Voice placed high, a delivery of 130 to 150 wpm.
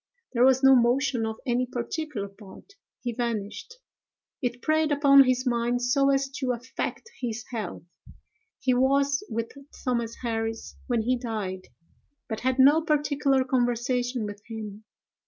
Yes: high, 245 Hz; average, 140 wpm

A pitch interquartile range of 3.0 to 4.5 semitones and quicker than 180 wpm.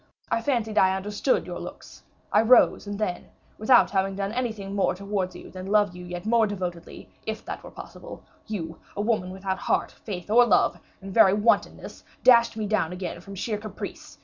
No: narrow, 2.6 semitones; average, 190 wpm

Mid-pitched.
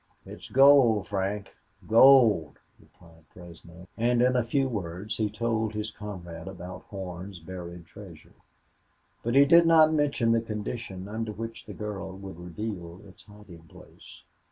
No: low, 105 Hz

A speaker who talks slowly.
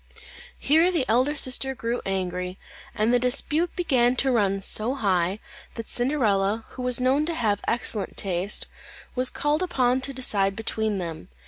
No: average, 155 wpm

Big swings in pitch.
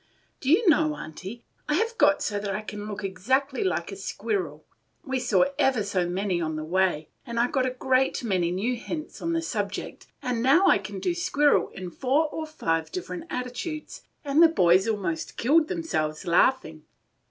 Yes: wide, 8.0 semitones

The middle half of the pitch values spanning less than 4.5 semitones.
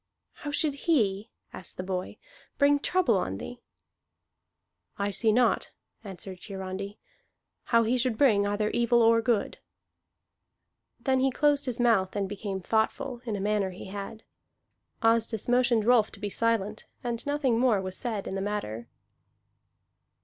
Yes: average, 3.8 semitones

